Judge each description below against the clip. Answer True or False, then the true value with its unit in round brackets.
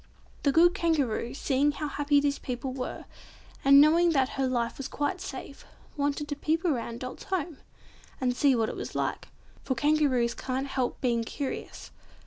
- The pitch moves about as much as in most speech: True (3.0 semitones)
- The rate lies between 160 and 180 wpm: True (165 wpm)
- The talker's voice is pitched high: True (280 Hz)